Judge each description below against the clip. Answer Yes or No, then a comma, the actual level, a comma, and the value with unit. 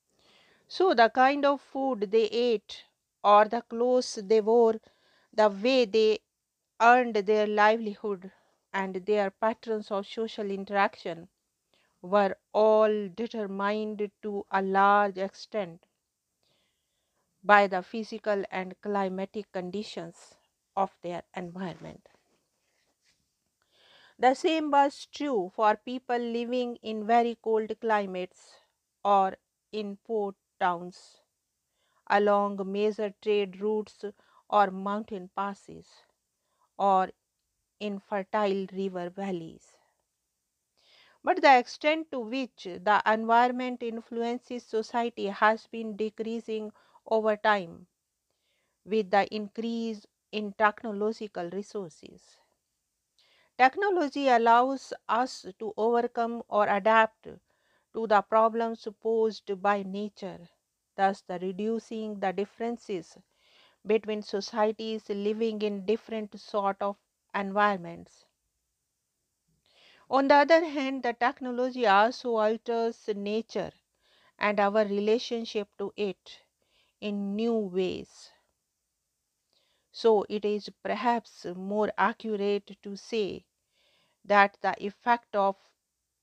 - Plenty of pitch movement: No, narrow, 2.4 semitones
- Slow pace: Yes, slow, 100 wpm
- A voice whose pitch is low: No, high, 215 Hz